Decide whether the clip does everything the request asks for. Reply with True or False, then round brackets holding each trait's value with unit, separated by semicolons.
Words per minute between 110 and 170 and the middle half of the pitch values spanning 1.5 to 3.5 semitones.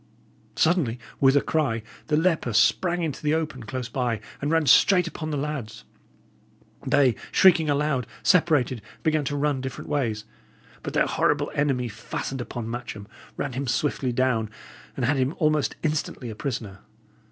False (160 wpm; 4.0 semitones)